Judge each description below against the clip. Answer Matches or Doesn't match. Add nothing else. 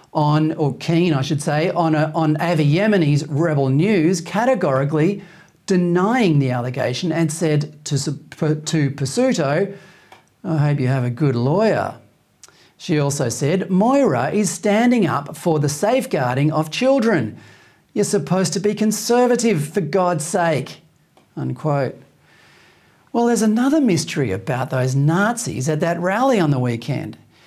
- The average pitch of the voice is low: Doesn't match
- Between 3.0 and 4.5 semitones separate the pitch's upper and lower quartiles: Doesn't match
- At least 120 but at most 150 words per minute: Matches